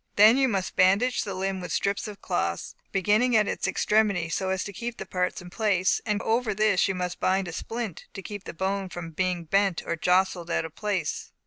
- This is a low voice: No, high, 195 Hz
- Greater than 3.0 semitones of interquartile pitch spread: No, narrow, 2.6 semitones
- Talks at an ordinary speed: No, fast, 220 wpm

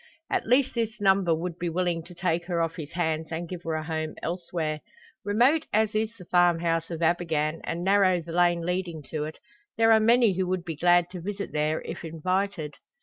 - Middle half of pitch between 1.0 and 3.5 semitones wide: Yes, average, 2.8 semitones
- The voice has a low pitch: No, medium, 175 Hz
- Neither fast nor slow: No, fast, 210 wpm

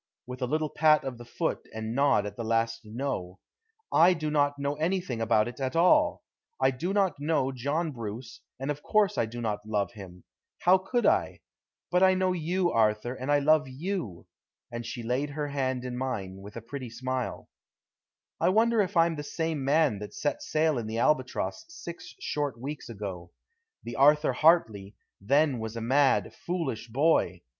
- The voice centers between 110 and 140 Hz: Yes, low, 135 Hz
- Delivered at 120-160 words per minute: No, average, 185 wpm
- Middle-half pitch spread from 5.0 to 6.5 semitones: Yes, wide, 5.6 semitones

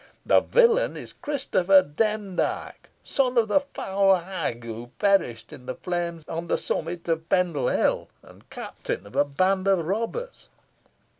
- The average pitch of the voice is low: No, medium, 185 Hz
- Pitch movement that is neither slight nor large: Yes, average, 4.7 semitones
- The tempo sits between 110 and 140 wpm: No, average, 150 wpm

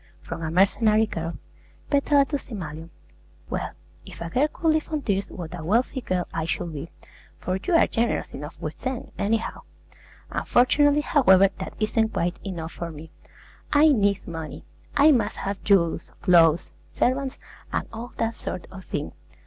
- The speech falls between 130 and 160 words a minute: No, average, 175 wpm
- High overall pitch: Yes, high, 200 Hz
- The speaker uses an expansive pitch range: Yes, wide, 7.3 semitones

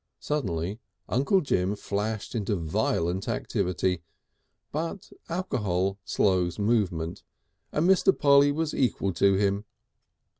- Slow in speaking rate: Yes, slow, 105 wpm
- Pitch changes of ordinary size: No, wide, 7.3 semitones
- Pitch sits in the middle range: No, low, 100 Hz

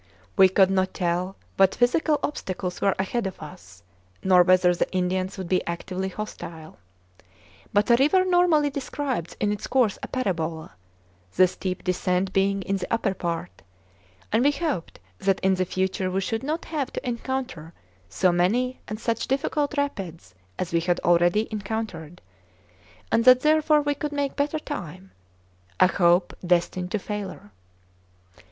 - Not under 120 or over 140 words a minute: No, average, 155 wpm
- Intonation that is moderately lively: No, wide, 6.0 semitones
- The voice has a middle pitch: No, high, 195 Hz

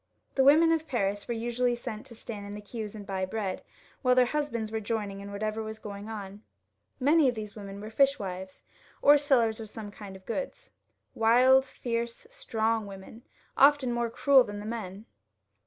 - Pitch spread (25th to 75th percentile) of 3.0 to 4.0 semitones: Yes, average, 3.5 semitones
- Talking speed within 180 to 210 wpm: Yes, average, 185 wpm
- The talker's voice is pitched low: No, high, 225 Hz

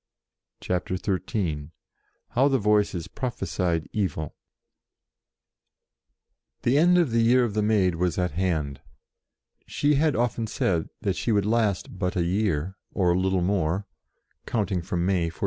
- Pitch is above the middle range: No, very low, 95 Hz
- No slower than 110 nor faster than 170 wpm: Yes, average, 145 wpm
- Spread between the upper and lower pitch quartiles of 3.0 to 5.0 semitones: Yes, average, 4.1 semitones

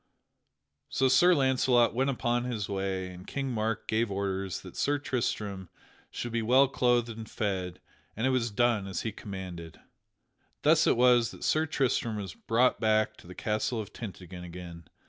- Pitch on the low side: Yes, low, 110 Hz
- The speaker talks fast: No, average, 170 wpm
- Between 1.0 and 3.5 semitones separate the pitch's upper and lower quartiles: No, average, 4.3 semitones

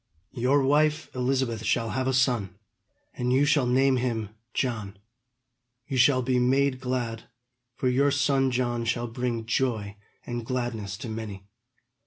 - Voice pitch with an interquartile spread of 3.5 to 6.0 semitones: No, narrow, 2.5 semitones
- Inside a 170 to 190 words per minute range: No, average, 145 wpm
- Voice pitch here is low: Yes, low, 125 Hz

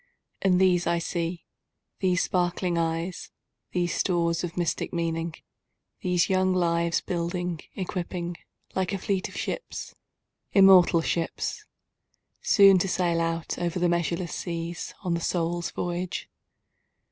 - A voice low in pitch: No, medium, 175 Hz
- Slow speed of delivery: Yes, slow, 100 wpm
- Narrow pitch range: Yes, narrow, 1.4 semitones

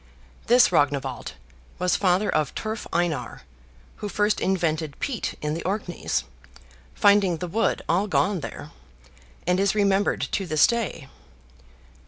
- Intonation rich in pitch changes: No, average, 4.1 semitones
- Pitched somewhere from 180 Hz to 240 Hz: Yes, medium, 185 Hz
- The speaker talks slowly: Yes, slow, 130 wpm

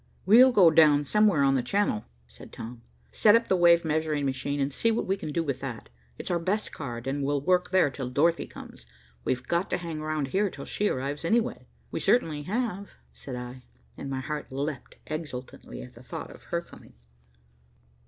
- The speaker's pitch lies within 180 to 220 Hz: No, medium, 150 Hz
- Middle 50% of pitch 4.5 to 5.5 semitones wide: Yes, average, 5.1 semitones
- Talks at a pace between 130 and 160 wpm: No, average, 200 wpm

